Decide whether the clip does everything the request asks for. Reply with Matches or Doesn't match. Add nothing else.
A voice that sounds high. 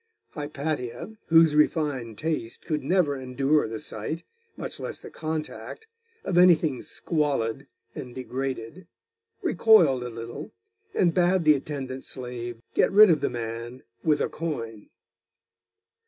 Doesn't match